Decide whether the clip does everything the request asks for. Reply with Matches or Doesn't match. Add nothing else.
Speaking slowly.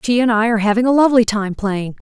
Doesn't match